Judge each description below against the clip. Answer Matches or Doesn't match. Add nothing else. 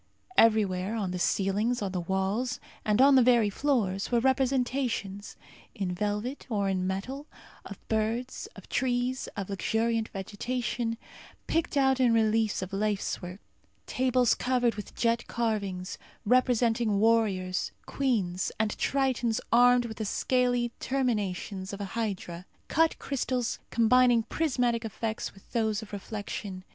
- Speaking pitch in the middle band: Doesn't match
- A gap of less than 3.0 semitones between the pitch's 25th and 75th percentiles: Doesn't match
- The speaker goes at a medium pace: Doesn't match